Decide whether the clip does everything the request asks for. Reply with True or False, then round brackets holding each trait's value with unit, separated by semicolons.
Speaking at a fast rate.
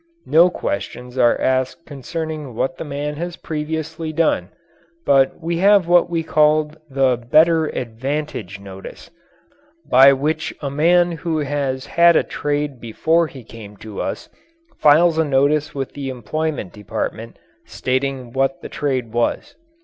False (140 wpm)